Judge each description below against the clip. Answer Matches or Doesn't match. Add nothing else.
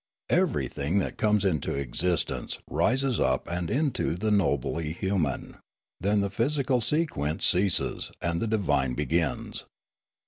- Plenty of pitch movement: Matches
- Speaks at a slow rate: Matches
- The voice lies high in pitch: Doesn't match